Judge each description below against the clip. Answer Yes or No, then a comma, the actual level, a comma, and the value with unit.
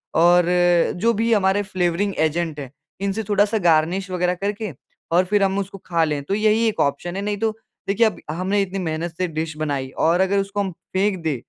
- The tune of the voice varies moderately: Yes, average, 3.3 semitones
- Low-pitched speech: No, medium, 185 Hz